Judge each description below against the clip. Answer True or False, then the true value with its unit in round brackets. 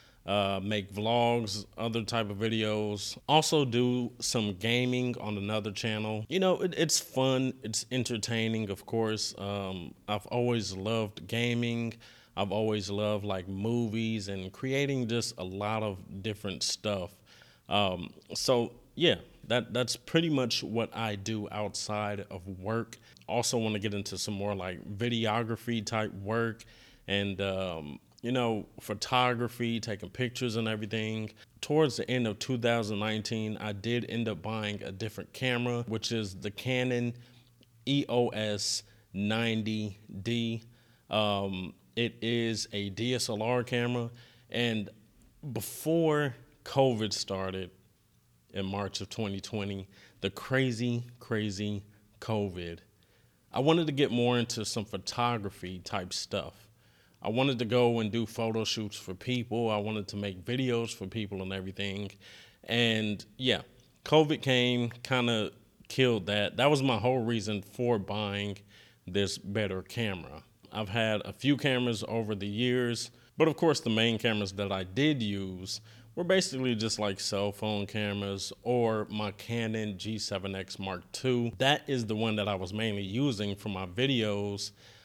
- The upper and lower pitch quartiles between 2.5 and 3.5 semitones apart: True (2.9 semitones)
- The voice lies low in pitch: True (110 Hz)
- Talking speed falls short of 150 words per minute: True (140 wpm)